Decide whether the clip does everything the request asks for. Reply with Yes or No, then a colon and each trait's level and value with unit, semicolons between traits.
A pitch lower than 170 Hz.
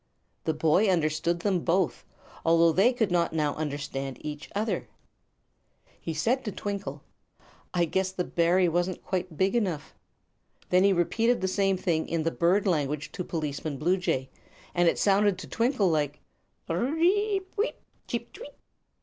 No: medium, 175 Hz